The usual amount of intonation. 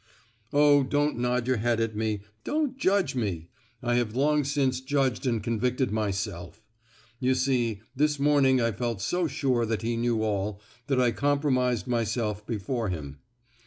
Yes: average, 4.0 semitones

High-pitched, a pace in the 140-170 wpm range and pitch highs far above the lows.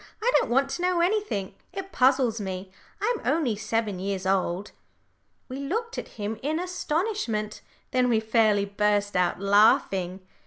Yes: high, 225 Hz; average, 150 wpm; wide, 8.0 semitones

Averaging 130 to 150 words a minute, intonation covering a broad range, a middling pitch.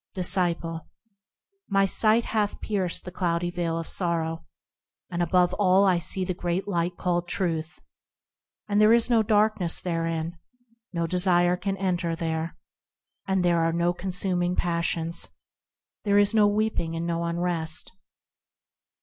No: average, 140 wpm; narrow, 2.4 semitones; medium, 175 Hz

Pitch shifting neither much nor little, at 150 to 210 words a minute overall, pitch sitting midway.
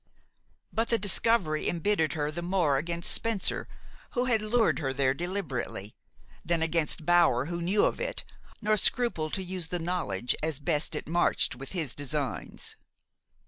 Yes: average, 4.7 semitones; average, 155 wpm; medium, 170 Hz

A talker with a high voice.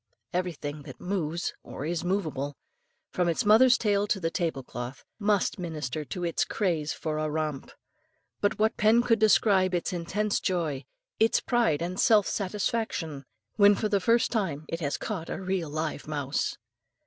No: medium, 175 Hz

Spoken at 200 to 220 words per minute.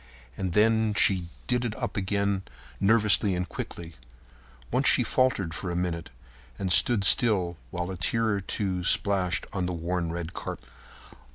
No: average, 160 wpm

